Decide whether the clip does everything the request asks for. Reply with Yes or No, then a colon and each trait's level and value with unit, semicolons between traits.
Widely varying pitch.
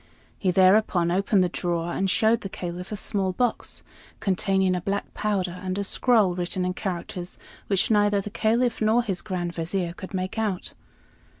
No: narrow, 2.5 semitones